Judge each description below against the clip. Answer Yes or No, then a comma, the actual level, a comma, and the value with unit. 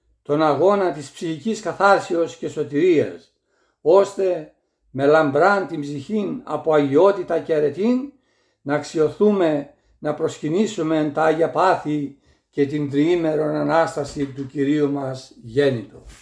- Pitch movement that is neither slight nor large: Yes, average, 4.0 semitones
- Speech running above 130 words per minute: No, slow, 115 wpm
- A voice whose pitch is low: No, medium, 155 Hz